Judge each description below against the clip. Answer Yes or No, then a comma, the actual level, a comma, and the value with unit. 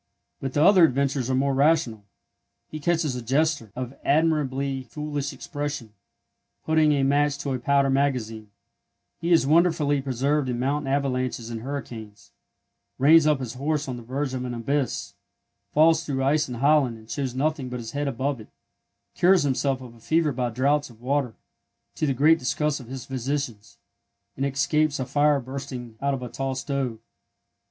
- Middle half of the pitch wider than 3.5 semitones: No, average, 2.7 semitones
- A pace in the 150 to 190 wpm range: Yes, average, 170 wpm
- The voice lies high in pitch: No, low, 135 Hz